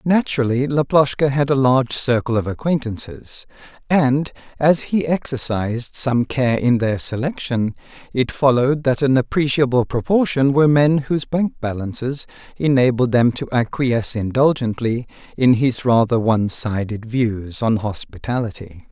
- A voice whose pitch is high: No, low, 125 Hz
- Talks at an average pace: No, slow, 130 wpm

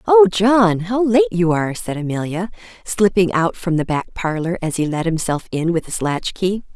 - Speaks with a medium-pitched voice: Yes, medium, 180 Hz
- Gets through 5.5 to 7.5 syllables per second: No, 4.9 syllables/s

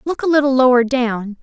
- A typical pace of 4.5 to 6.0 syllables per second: Yes, 5.3 syllables/s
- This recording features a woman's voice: Yes, female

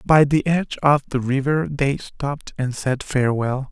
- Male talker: Yes, male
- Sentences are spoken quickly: No, average, 175 wpm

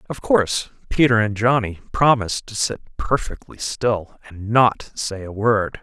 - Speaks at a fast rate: No, average, 155 wpm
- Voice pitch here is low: Yes, low, 110 Hz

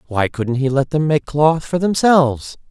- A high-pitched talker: No, medium, 145 Hz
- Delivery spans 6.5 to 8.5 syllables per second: No, 4.5 syllables/s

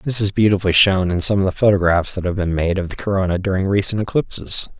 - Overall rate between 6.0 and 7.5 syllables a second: Yes, 6.4 syllables/s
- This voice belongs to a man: Yes, male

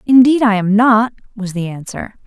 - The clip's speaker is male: No, female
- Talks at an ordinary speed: Yes, average, 185 wpm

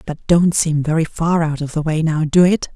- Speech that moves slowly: No, fast, 260 wpm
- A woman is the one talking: No, male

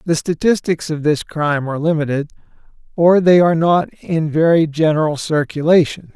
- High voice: No, medium, 160 Hz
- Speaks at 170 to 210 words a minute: No, average, 145 wpm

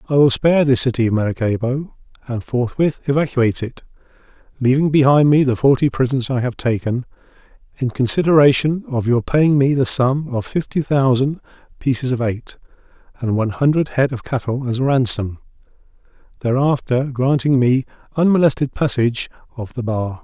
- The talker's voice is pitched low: Yes, low, 130 Hz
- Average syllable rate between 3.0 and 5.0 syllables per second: No, 5.4 syllables/s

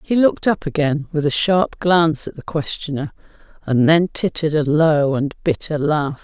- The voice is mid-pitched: Yes, medium, 155 Hz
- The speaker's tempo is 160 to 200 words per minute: Yes, average, 185 wpm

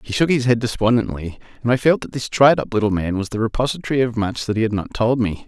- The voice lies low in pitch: Yes, low, 115 Hz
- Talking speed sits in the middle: No, fast, 275 wpm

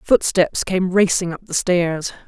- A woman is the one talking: Yes, female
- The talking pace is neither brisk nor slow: Yes, average, 160 wpm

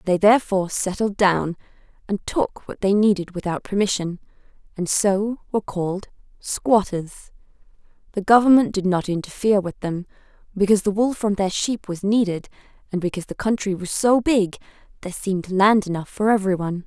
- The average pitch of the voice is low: No, high, 200 Hz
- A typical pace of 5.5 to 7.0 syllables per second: Yes, 5.6 syllables/s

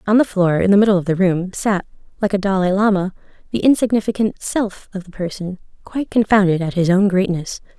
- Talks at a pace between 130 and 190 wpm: No, average, 200 wpm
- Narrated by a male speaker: No, female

